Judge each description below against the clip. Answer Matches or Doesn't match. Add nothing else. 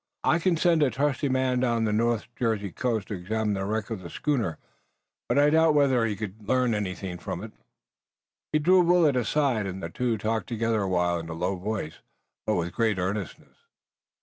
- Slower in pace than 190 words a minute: Doesn't match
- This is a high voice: Doesn't match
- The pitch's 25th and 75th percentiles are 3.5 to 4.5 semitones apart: Doesn't match